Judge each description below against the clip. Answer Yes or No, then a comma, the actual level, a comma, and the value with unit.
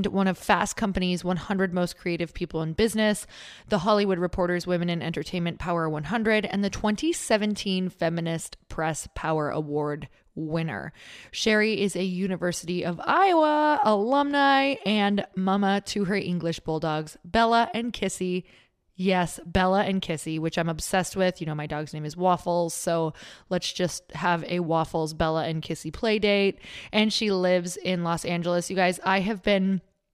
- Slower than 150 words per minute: No, average, 155 wpm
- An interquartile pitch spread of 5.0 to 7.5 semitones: No, average, 3.4 semitones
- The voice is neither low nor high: Yes, medium, 180 Hz